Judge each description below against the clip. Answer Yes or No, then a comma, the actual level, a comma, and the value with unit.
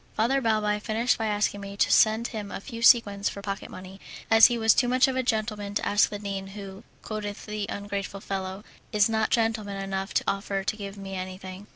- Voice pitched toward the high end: Yes, high, 205 Hz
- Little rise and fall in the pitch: Yes, narrow, 2.0 semitones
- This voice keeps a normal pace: No, fast, 215 wpm